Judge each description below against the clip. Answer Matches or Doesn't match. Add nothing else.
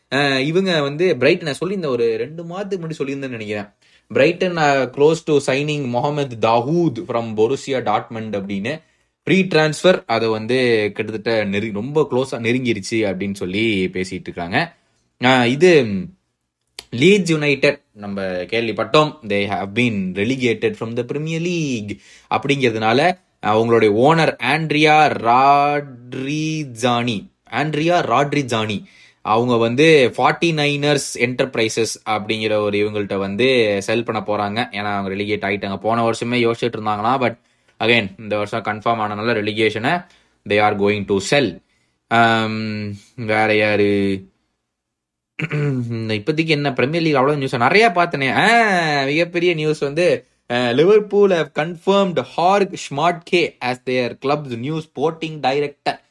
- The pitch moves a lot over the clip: Matches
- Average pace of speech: Matches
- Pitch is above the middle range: Doesn't match